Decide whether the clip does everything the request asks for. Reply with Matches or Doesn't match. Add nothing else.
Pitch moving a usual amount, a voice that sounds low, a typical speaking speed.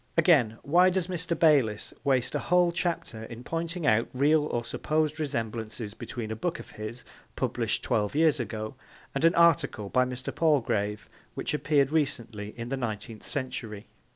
Doesn't match